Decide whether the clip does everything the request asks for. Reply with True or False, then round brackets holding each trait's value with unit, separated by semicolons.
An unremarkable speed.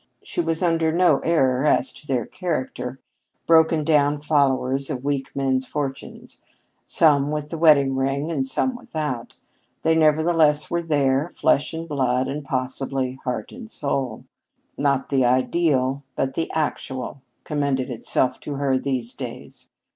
True (145 wpm)